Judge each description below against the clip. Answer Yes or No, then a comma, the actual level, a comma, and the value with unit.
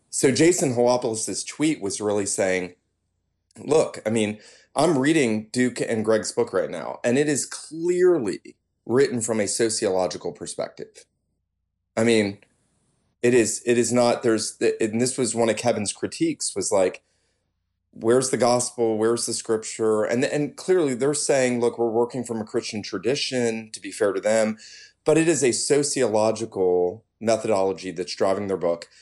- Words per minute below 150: No, average, 160 wpm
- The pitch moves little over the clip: No, average, 3.2 semitones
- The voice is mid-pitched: No, low, 115 Hz